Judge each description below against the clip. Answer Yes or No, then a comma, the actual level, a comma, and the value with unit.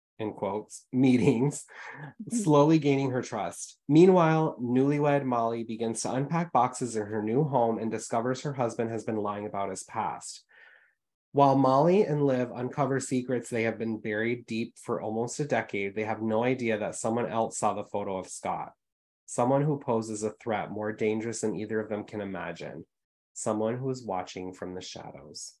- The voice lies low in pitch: Yes, low, 115 Hz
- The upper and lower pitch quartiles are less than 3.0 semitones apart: No, average, 3.7 semitones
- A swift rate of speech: No, average, 175 wpm